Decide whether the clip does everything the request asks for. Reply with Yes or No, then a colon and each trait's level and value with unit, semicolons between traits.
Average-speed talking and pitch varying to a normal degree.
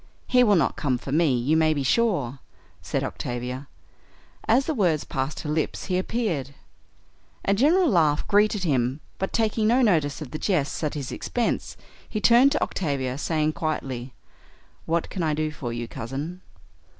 No: average, 170 wpm; wide, 7.1 semitones